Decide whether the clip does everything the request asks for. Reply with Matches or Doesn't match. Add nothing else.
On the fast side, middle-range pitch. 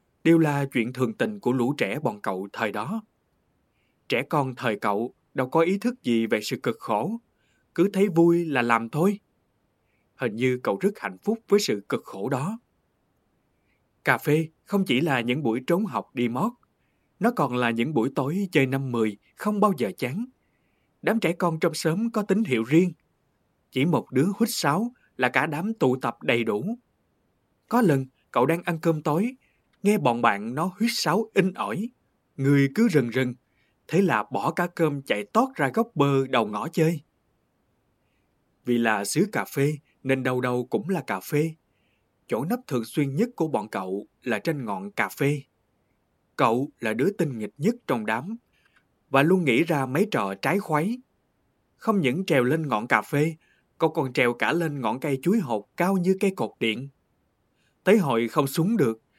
Doesn't match